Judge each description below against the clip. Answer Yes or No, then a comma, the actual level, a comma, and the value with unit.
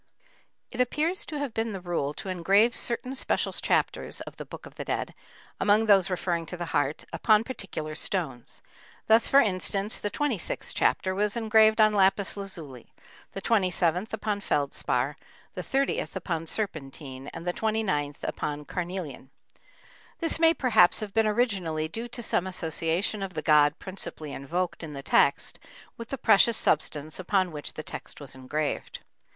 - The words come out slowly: No, average, 165 wpm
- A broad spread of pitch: Yes, wide, 5.9 semitones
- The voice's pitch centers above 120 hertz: Yes, high, 190 Hz